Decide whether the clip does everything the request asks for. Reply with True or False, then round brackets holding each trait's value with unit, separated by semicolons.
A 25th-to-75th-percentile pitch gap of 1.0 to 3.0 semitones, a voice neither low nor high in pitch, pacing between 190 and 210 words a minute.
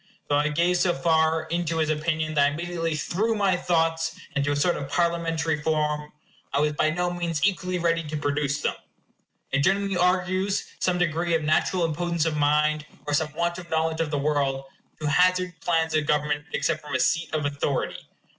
True (2.5 semitones; 160 Hz; 195 wpm)